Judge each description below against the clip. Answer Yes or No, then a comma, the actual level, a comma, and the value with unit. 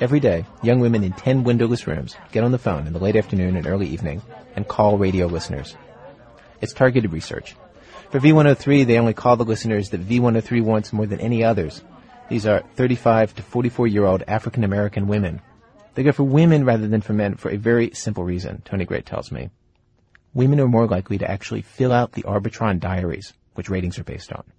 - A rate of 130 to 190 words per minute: No, fast, 205 wpm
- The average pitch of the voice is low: Yes, low, 110 Hz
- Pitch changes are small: No, average, 3.6 semitones